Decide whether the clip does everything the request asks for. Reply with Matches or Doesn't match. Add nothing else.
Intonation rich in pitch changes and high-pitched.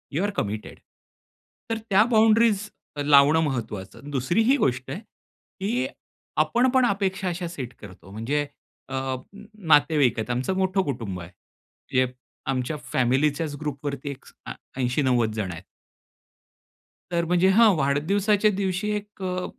Doesn't match